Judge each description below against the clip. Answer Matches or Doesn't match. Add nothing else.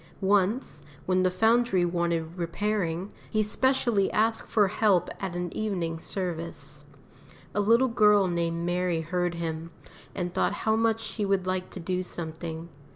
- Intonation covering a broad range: Doesn't match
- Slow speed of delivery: Doesn't match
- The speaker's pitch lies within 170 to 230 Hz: Matches